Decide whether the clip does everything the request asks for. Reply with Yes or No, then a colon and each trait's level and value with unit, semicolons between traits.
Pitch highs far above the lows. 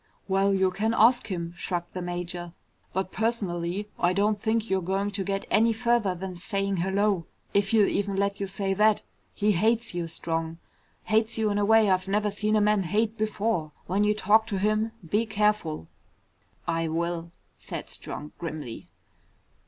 No: average, 3.2 semitones